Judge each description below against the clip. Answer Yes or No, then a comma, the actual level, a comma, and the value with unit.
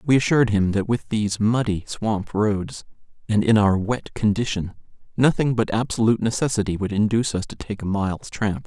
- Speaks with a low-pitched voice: Yes, low, 110 Hz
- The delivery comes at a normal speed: Yes, average, 180 wpm